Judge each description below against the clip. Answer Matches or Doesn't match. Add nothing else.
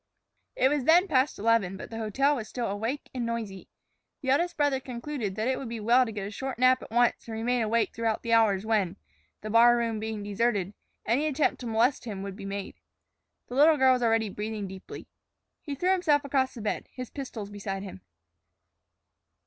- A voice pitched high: Matches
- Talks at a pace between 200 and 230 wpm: Matches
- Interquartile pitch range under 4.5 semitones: Matches